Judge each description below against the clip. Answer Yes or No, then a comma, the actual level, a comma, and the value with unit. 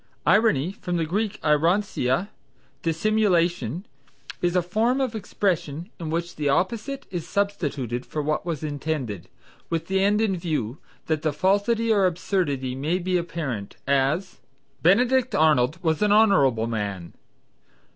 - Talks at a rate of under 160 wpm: Yes, slow, 135 wpm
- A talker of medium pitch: Yes, medium, 170 Hz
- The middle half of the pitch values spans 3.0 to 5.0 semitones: No, wide, 5.6 semitones